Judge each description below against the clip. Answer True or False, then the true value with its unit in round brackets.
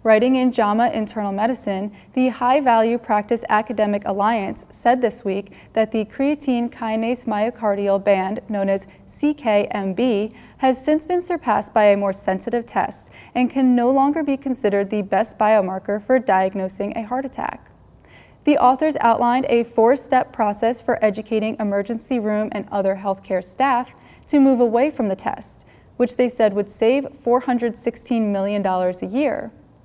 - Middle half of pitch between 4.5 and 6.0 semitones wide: False (3.4 semitones)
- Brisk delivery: False (155 wpm)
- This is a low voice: False (225 Hz)